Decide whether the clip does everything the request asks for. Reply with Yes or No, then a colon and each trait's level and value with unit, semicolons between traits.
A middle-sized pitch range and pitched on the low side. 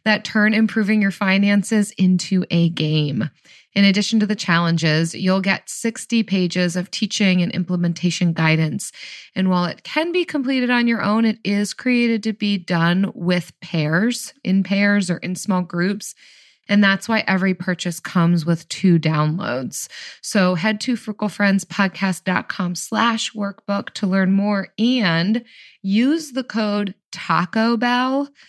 No: average, 3.5 semitones; high, 200 Hz